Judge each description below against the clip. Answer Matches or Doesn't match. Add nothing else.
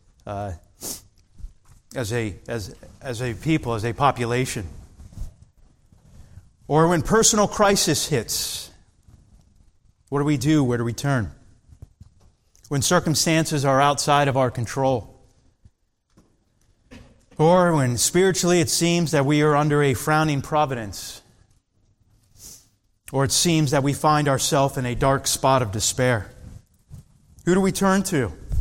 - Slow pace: Matches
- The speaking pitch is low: Matches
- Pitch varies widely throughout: Matches